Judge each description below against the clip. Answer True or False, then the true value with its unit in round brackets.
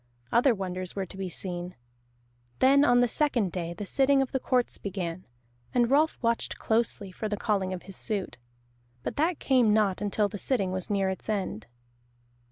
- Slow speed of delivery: False (180 wpm)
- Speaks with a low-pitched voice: False (205 Hz)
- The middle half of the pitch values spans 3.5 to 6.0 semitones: True (4.7 semitones)